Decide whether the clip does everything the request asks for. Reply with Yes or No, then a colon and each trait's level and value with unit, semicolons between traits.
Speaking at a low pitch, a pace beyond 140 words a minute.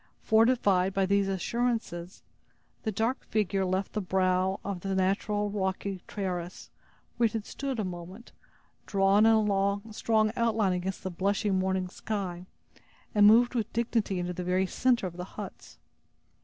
No: high, 195 Hz; average, 155 wpm